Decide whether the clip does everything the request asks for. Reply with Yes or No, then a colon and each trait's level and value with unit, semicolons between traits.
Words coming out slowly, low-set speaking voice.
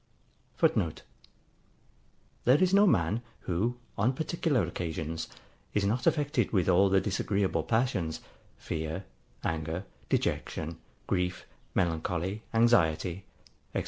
Yes: slow, 105 wpm; very low, 95 Hz